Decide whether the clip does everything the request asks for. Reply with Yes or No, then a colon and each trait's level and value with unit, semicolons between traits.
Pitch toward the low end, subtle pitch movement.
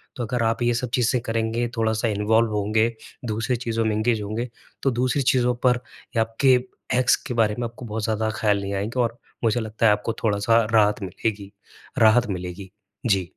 Yes: low, 115 Hz; narrow, 2.1 semitones